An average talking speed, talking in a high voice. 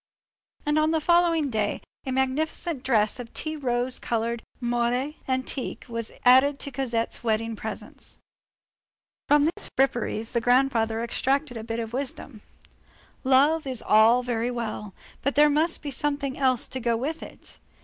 Yes: average, 150 wpm; very high, 255 Hz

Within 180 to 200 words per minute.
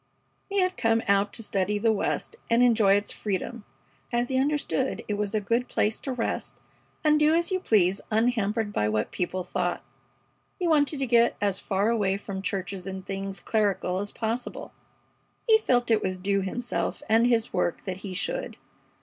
Yes: average, 185 wpm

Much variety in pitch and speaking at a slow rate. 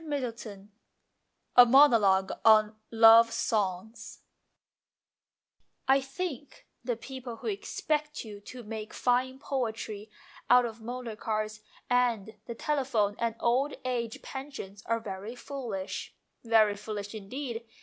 No: average, 3.1 semitones; slow, 120 wpm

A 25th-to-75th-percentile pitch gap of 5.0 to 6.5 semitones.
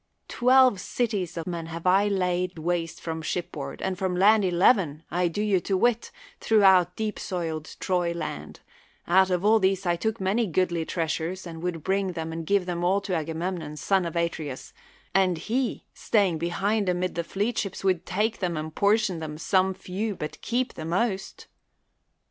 No: average, 2.9 semitones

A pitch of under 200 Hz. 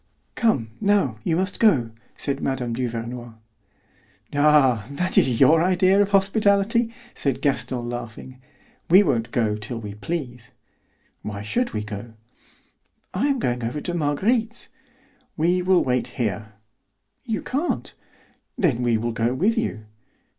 Yes: low, 135 Hz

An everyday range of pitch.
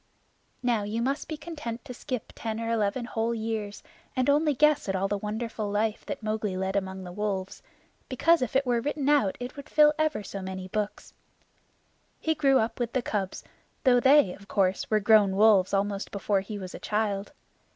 Yes: average, 4.4 semitones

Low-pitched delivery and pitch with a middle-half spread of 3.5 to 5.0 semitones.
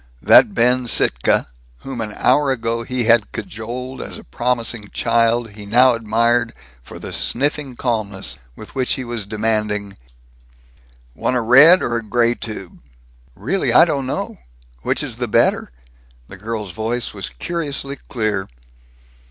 No: low, 115 Hz; average, 2.9 semitones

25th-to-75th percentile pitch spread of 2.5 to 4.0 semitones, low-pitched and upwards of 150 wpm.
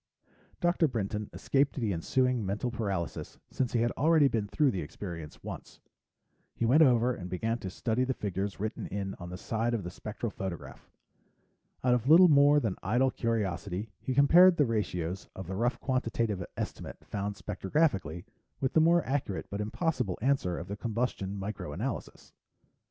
No: average, 5.2 semitones; low, 115 Hz; average, 170 wpm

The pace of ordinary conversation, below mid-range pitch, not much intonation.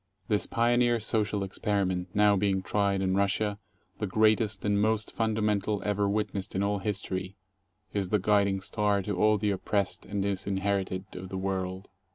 Yes: average, 170 wpm; low, 100 Hz; narrow, 1.7 semitones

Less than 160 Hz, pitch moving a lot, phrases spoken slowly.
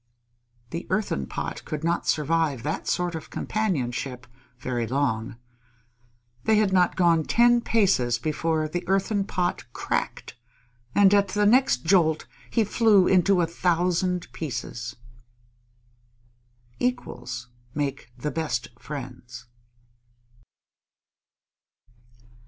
No: medium, 165 Hz; wide, 6.9 semitones; slow, 105 wpm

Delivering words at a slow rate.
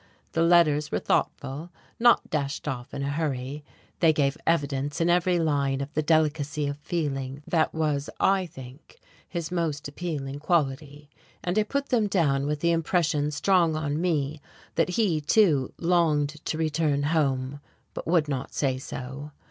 No: average, 160 wpm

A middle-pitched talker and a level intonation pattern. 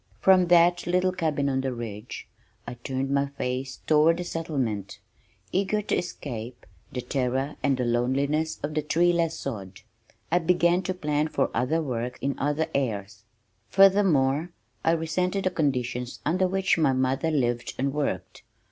No: medium, 145 Hz; average, 5.2 semitones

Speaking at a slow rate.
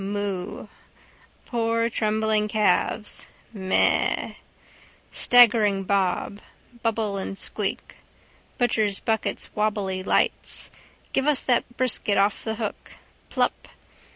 Yes: slow, 95 wpm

